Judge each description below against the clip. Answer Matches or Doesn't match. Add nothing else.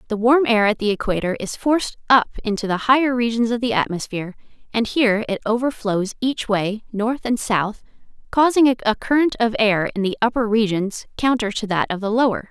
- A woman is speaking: Matches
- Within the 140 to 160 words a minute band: Doesn't match